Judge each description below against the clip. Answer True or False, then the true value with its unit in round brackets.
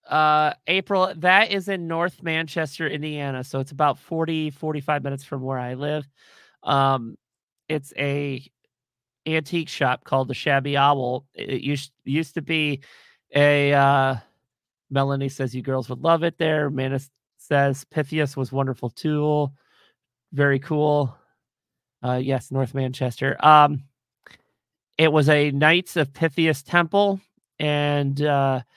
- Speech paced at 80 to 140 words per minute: True (135 wpm)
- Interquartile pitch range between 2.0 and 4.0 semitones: True (2.6 semitones)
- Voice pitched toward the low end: False (145 Hz)